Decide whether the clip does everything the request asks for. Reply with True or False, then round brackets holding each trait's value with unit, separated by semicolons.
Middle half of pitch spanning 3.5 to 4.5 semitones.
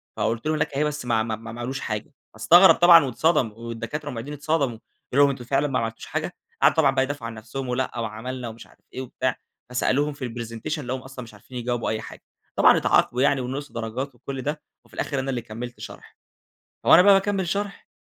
True (3.8 semitones)